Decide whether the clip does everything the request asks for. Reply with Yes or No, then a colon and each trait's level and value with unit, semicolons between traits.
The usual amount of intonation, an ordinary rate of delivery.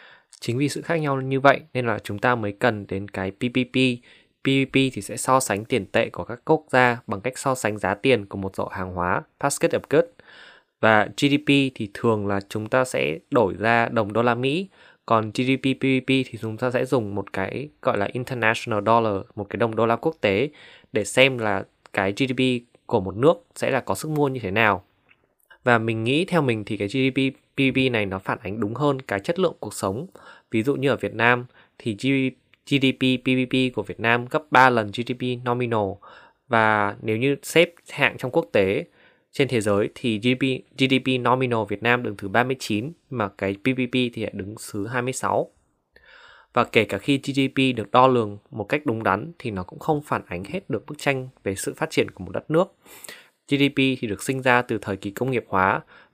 Yes: average, 3.8 semitones; average, 210 wpm